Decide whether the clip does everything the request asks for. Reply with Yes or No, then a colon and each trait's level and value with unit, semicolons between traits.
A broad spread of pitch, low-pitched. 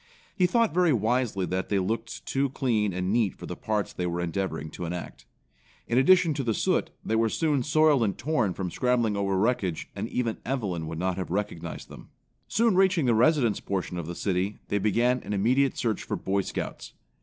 Yes: wide, 5.7 semitones; low, 110 Hz